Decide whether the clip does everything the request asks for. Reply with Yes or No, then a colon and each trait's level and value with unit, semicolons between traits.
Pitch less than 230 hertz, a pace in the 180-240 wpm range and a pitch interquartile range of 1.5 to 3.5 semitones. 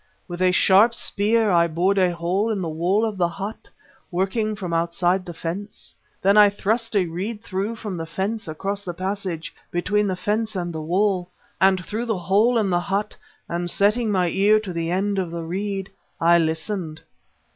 Yes: high, 190 Hz; average, 190 wpm; average, 3.1 semitones